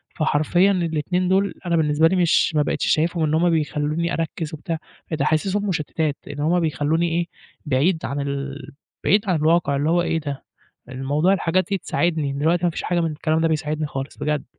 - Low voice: No, medium, 160 Hz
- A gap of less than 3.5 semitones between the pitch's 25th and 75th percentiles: Yes, average, 2.7 semitones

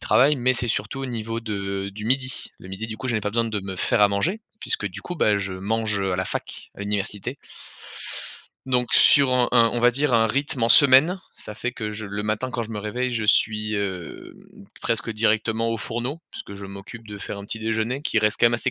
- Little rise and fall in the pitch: No, average, 3.1 semitones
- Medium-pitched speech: No, low, 110 Hz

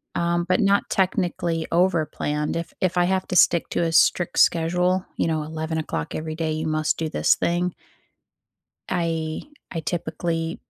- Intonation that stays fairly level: Yes, narrow, 2.0 semitones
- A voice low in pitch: No, medium, 165 Hz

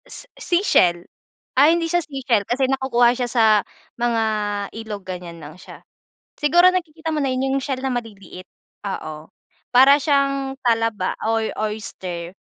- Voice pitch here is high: Yes, high, 245 Hz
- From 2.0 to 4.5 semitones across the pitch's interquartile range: No, average, 5.0 semitones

